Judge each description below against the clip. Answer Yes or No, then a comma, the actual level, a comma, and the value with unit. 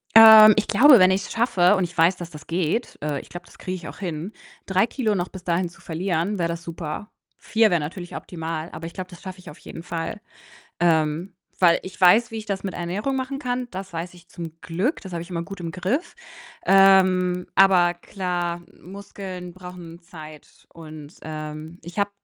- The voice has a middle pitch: Yes, medium, 180 Hz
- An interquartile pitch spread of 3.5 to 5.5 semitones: No, average, 2.7 semitones